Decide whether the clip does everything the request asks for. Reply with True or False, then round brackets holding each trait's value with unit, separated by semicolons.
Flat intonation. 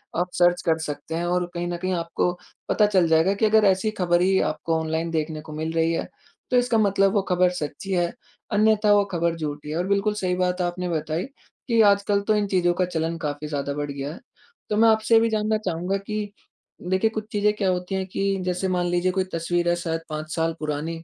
False (3.5 semitones)